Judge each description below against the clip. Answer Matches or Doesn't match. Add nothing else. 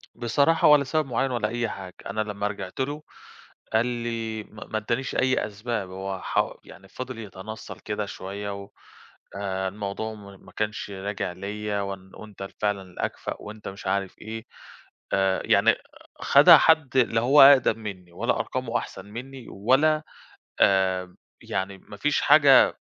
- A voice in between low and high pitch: Doesn't match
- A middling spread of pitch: Matches